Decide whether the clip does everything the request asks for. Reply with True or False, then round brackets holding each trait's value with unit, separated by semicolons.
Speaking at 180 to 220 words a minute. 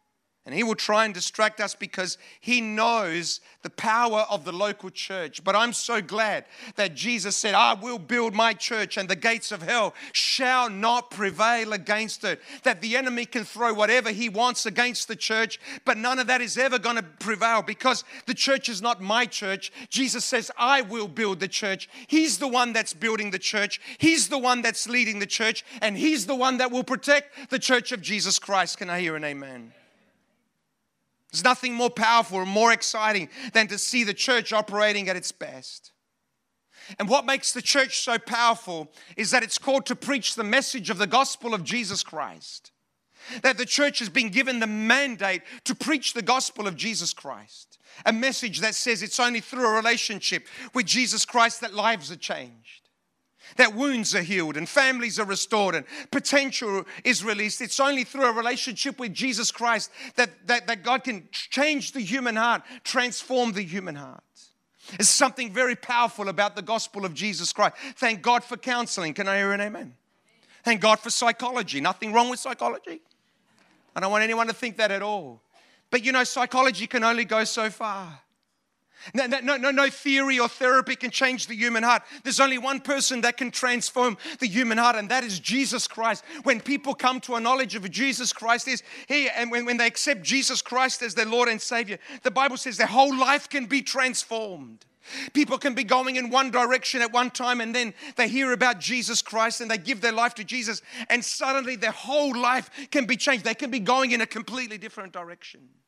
True (200 wpm)